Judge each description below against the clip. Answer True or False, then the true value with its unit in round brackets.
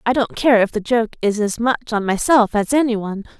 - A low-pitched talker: False (225 Hz)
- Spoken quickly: True (250 wpm)